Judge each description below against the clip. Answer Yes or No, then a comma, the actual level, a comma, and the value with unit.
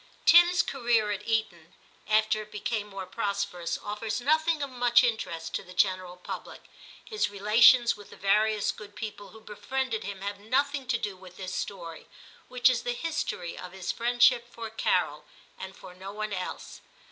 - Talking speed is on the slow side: No, average, 170 wpm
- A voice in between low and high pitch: No, high, 215 Hz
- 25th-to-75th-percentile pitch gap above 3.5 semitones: Yes, average, 3.9 semitones